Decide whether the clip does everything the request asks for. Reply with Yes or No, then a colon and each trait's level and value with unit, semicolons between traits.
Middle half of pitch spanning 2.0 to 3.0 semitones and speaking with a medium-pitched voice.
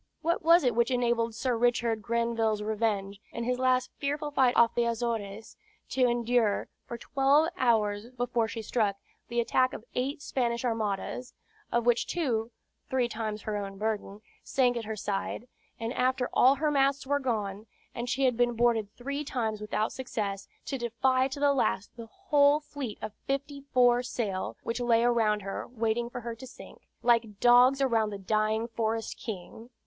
No: average, 2.7 semitones; high, 235 Hz